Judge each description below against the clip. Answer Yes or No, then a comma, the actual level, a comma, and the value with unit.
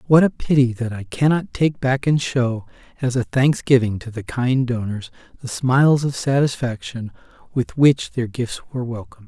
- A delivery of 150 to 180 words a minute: Yes, average, 175 wpm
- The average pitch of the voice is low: Yes, low, 125 Hz